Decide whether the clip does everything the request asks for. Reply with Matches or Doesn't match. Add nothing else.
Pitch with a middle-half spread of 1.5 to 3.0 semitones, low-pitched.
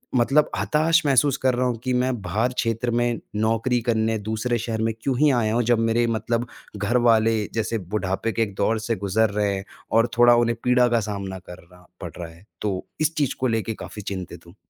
Matches